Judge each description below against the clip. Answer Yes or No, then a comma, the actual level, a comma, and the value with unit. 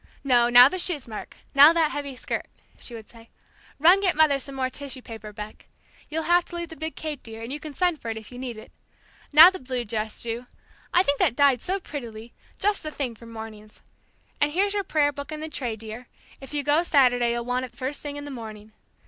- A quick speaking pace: Yes, fast, 240 wpm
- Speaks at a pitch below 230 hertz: No, very high, 270 Hz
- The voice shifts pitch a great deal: No, average, 4.8 semitones